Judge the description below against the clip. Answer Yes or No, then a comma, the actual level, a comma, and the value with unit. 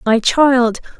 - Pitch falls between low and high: No, high, 245 Hz